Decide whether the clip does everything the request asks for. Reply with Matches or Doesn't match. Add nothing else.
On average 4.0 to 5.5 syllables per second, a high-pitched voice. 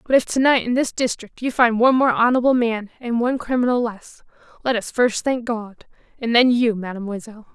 Doesn't match